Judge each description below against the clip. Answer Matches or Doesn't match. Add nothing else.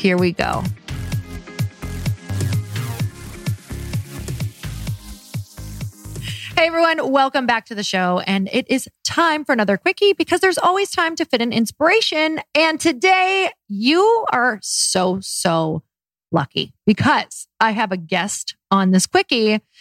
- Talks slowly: Matches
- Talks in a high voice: Matches